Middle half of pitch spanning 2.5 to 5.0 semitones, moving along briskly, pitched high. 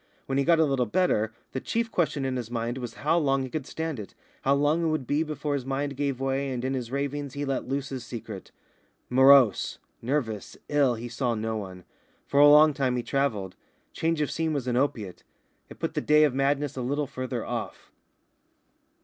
No: average, 3.0 semitones; fast, 210 wpm; low, 135 Hz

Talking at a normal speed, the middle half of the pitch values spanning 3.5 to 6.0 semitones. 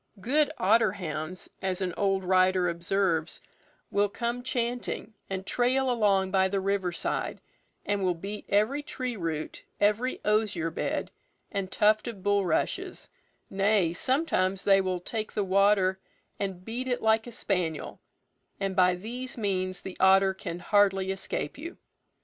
No: average, 145 wpm; average, 2.9 semitones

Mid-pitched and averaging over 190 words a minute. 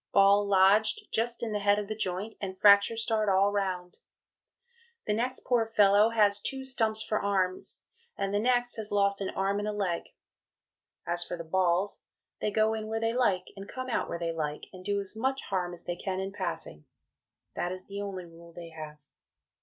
No: high, 200 Hz; average, 200 wpm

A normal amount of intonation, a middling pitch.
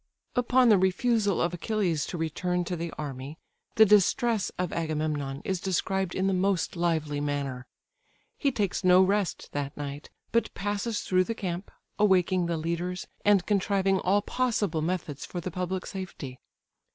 Yes: average, 3.8 semitones; medium, 180 Hz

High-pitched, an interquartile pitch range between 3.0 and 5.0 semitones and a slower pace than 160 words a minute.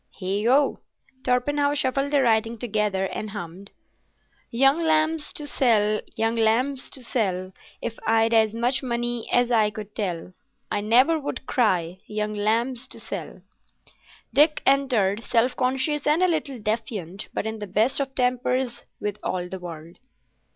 Yes: high, 230 Hz; average, 4.1 semitones; average, 150 wpm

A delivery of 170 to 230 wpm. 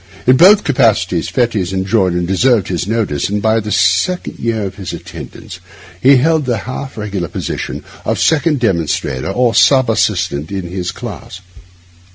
No: average, 160 wpm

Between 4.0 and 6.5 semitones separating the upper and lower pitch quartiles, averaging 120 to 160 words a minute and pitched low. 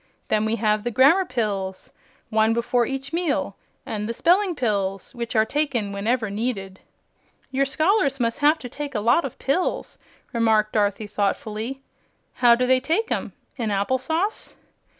No: average, 4.5 semitones; average, 155 wpm; high, 235 Hz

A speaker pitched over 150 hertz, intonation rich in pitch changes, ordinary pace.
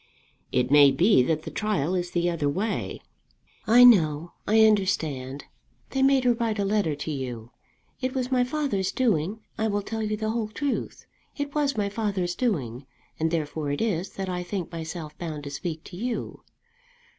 Yes: high, 190 Hz; wide, 6.3 semitones; average, 180 wpm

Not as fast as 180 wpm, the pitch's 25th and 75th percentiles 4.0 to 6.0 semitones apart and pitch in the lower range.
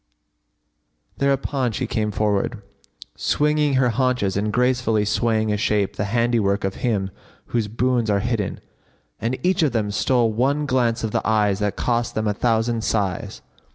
No: average, 160 wpm; average, 3.2 semitones; low, 115 Hz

